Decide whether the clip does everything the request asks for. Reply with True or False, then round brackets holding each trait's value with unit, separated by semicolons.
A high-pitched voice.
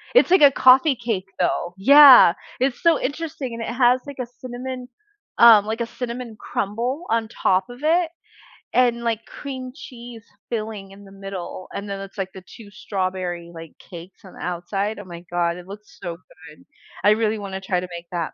True (220 Hz)